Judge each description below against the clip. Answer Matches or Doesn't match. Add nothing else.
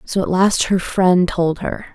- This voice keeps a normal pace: Doesn't match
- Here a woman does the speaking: Matches